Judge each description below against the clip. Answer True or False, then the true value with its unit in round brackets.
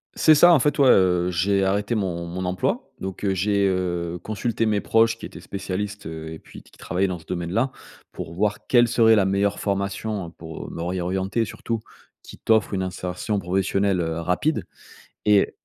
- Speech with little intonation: False (3.0 semitones)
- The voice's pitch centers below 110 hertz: True (95 Hz)